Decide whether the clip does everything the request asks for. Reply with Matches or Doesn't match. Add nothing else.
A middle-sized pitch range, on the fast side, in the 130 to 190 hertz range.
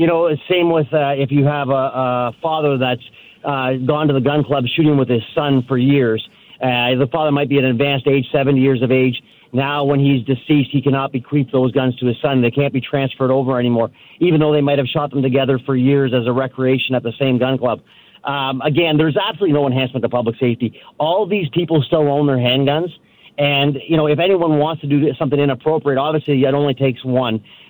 Doesn't match